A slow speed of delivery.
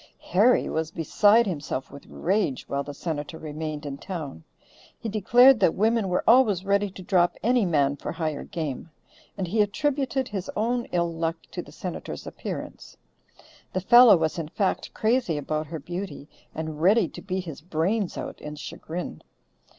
No: average, 165 wpm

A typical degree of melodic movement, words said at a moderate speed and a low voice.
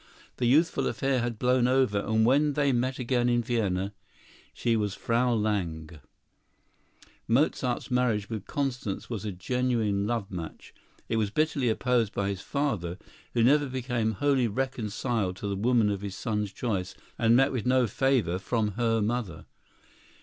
Yes: average, 3.7 semitones; average, 155 wpm; low, 115 Hz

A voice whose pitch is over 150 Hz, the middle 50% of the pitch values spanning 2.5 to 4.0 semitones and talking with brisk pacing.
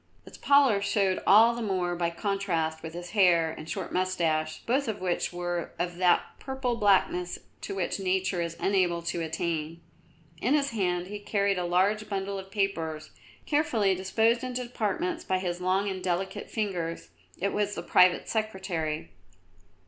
No: high, 190 Hz; average, 3.1 semitones; average, 165 wpm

